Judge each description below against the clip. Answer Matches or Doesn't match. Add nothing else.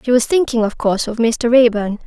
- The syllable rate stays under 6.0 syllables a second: Matches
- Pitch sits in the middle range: Doesn't match